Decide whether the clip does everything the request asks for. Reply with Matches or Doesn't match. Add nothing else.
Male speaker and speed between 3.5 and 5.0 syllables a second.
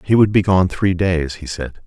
Matches